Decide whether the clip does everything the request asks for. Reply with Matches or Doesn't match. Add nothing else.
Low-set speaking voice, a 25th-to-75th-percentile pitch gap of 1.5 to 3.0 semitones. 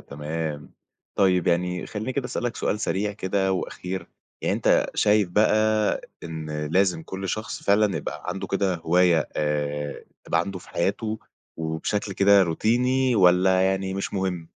Doesn't match